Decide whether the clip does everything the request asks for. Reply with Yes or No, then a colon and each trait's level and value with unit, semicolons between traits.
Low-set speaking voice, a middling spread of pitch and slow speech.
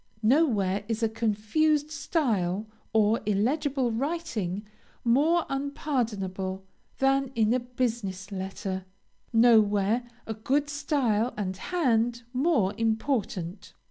No: high, 230 Hz; average, 4.9 semitones; slow, 100 wpm